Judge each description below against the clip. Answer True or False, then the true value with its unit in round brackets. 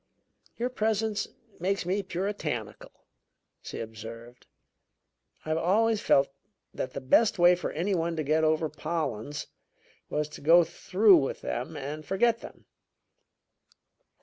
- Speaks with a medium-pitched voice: True (165 Hz)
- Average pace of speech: False (130 wpm)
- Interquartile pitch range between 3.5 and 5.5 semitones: True (5.2 semitones)